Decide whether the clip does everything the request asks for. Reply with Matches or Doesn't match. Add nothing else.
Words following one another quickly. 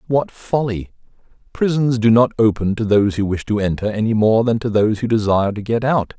Matches